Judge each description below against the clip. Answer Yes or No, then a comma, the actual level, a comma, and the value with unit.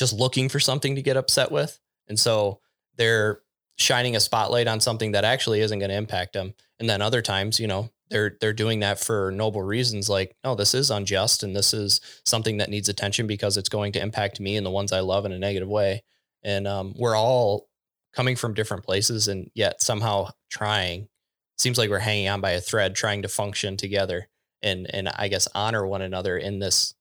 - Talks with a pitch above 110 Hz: No, low, 105 Hz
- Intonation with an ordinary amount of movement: No, narrow, 2.2 semitones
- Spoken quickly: Yes, fast, 215 wpm